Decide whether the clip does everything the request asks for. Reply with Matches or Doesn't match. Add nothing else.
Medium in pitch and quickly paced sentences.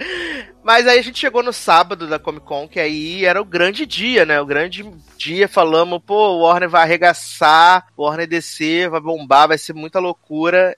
Matches